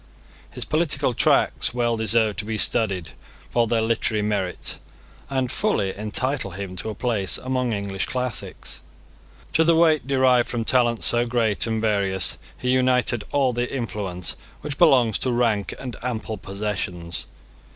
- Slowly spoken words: No, average, 150 wpm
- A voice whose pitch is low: Yes, low, 115 Hz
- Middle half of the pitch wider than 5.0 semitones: No, average, 3.6 semitones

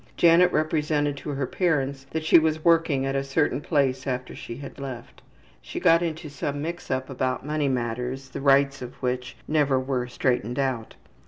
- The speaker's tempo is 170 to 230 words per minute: Yes, average, 180 wpm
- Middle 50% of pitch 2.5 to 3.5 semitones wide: Yes, average, 2.9 semitones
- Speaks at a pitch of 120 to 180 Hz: Yes, medium, 140 Hz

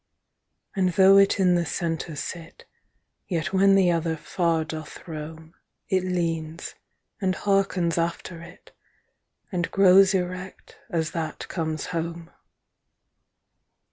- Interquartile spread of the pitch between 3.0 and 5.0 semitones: No, narrow, 2.4 semitones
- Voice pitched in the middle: Yes, medium, 170 Hz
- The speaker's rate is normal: No, slow, 120 wpm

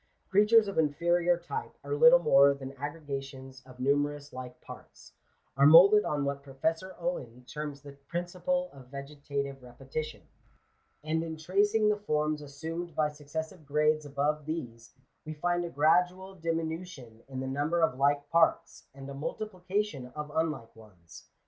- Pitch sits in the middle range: Yes, medium, 150 Hz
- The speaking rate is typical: Yes, average, 155 wpm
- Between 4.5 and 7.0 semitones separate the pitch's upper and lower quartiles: No, average, 3.9 semitones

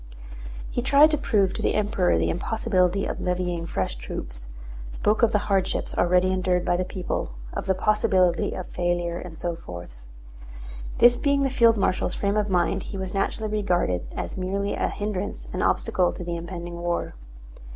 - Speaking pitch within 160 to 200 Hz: Yes, medium, 185 Hz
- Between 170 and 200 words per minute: Yes, average, 175 wpm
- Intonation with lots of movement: No, average, 3.1 semitones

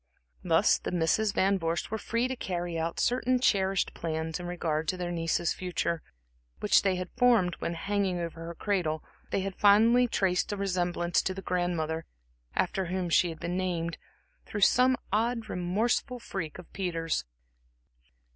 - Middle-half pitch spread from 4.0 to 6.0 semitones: No, average, 3.3 semitones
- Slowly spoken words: No, average, 165 wpm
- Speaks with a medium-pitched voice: Yes, medium, 180 Hz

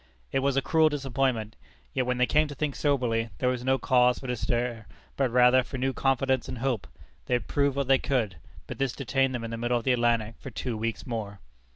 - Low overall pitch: Yes, low, 125 Hz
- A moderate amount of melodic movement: No, narrow, 2.3 semitones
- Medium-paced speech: No, fast, 235 wpm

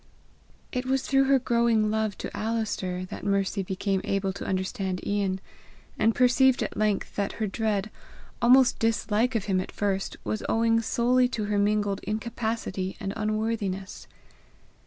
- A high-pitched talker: Yes, high, 215 Hz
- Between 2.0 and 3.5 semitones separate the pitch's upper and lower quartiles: Yes, average, 2.8 semitones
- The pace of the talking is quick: No, average, 150 wpm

